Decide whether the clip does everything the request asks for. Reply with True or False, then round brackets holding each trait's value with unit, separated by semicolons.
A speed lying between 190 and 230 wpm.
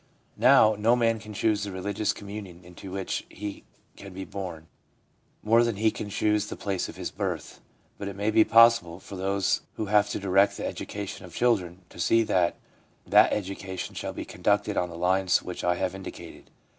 True (195 wpm)